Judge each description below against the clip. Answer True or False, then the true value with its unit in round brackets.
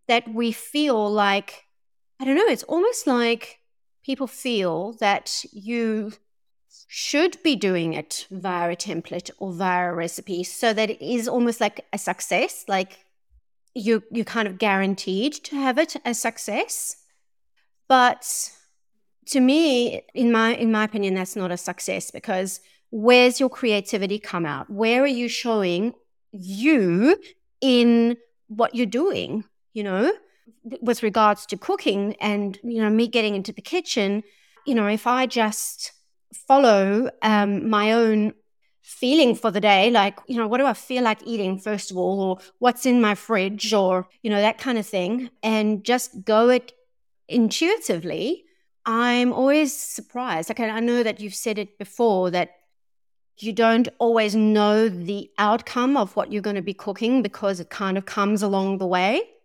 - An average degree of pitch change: True (3.6 semitones)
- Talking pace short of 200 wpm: True (165 wpm)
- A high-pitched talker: True (220 Hz)